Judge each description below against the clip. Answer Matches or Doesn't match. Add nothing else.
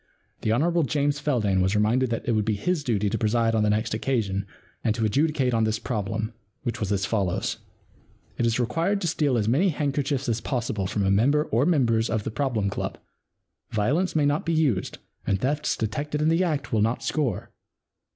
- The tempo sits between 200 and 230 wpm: Matches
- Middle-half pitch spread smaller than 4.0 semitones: Doesn't match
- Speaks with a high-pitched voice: Doesn't match